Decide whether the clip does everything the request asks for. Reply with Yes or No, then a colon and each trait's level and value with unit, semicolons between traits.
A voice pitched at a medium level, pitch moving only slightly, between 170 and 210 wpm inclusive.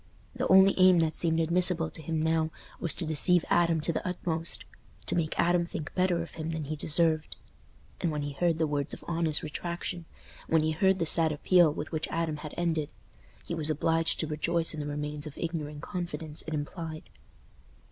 Yes: medium, 160 Hz; narrow, 1.8 semitones; average, 190 wpm